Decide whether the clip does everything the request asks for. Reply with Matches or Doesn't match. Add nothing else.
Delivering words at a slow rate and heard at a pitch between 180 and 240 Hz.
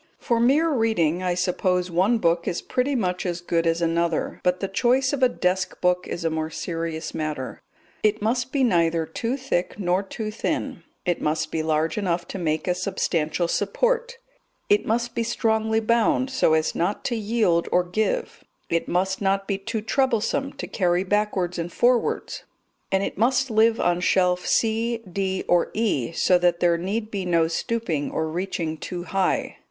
Doesn't match